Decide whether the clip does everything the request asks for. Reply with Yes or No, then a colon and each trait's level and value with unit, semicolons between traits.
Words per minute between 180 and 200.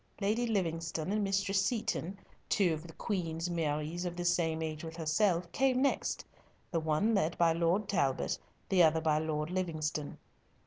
No: average, 165 wpm